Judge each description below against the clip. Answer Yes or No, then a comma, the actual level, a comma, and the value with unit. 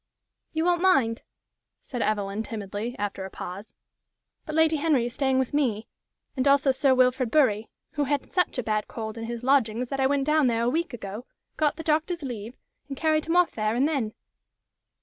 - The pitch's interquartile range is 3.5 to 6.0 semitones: Yes, average, 5.0 semitones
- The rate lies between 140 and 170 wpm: No, average, 195 wpm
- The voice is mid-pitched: No, very high, 260 Hz